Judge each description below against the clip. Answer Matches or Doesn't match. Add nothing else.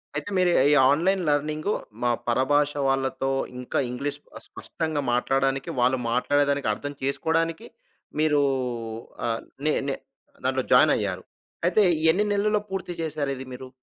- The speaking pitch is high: Doesn't match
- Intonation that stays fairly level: Doesn't match